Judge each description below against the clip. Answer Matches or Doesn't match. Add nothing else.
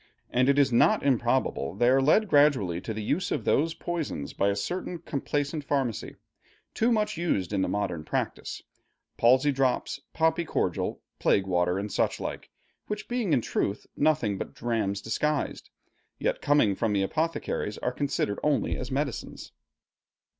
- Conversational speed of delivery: Matches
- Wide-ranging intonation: Matches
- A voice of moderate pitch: Doesn't match